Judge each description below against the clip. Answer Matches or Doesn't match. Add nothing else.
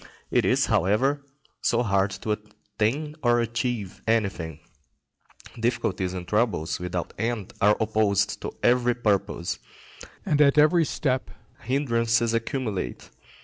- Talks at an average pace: Doesn't match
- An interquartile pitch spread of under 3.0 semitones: Doesn't match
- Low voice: Matches